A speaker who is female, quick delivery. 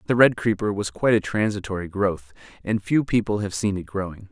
No: male; fast, 210 wpm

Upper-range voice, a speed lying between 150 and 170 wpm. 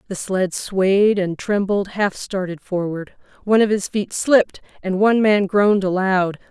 Yes: high, 195 Hz; average, 165 wpm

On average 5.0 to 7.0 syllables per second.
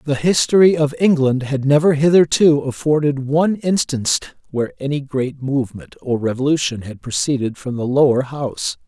Yes: 5.3 syllables/s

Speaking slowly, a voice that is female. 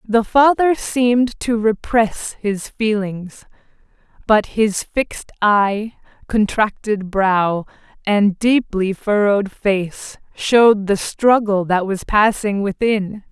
Yes: slow, 110 wpm; female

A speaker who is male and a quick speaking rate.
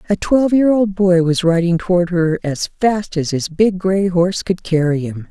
No: female; fast, 215 wpm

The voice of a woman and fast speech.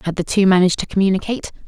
Yes: female; fast, 215 wpm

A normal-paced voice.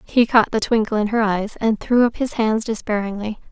No: fast, 220 wpm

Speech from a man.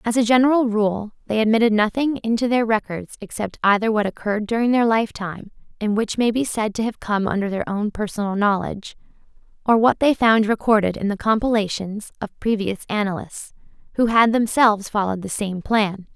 No: female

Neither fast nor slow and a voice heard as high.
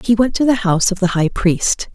No: fast, 275 wpm; high, 205 Hz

